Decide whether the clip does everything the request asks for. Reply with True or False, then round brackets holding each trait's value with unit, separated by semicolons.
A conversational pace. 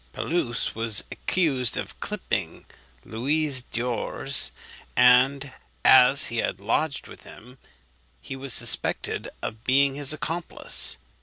False (110 wpm)